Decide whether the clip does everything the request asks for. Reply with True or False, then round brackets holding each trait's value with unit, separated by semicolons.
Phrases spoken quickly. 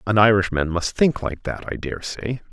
False (190 wpm)